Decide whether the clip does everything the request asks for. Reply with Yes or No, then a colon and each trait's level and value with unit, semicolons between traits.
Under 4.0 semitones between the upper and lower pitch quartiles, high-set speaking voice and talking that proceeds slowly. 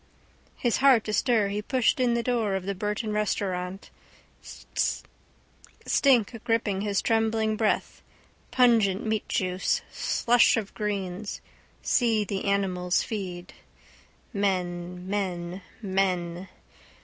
Yes: average, 3.1 semitones; high, 205 Hz; slow, 100 wpm